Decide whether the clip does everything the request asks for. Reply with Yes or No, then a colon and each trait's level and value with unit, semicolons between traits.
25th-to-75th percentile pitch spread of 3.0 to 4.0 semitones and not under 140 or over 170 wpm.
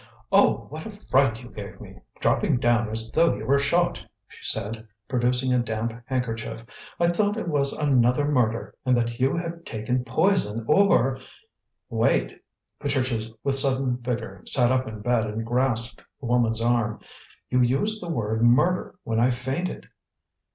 Yes: average, 3.4 semitones; average, 165 wpm